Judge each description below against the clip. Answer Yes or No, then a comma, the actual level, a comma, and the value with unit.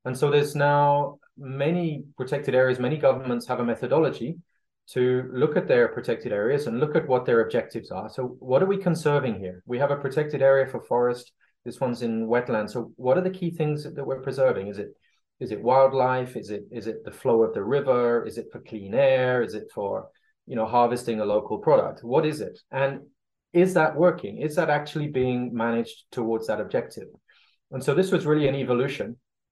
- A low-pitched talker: Yes, low, 130 Hz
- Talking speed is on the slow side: No, fast, 205 wpm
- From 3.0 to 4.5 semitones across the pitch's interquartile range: Yes, average, 3.8 semitones